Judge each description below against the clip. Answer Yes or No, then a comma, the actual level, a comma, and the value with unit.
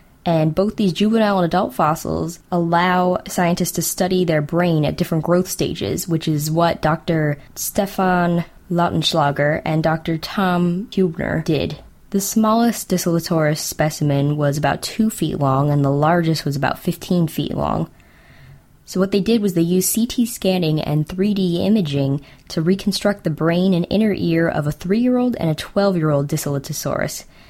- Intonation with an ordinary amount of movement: Yes, average, 3.7 semitones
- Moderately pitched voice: Yes, medium, 170 Hz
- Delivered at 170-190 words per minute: No, average, 155 wpm